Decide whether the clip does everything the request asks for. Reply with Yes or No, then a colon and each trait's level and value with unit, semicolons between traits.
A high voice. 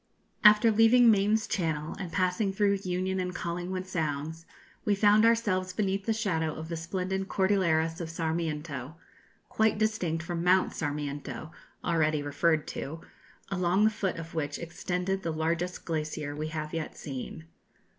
No: medium, 175 Hz